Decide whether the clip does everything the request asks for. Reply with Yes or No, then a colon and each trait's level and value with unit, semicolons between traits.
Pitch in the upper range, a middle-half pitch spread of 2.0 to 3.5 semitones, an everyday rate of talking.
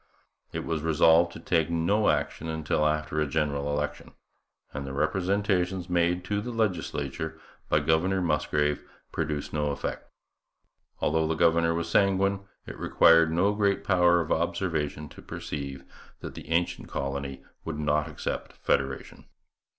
No: very low, 80 Hz; average, 3.0 semitones; average, 145 wpm